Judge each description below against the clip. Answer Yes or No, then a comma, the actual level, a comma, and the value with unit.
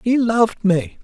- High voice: Yes, high, 205 Hz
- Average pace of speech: Yes, average, 175 wpm